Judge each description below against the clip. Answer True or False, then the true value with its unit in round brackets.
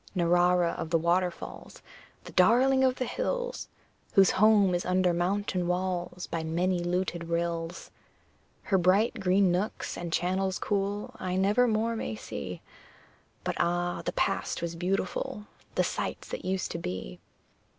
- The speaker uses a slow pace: False (145 wpm)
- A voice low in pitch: False (180 Hz)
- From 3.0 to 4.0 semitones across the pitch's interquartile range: False (2.5 semitones)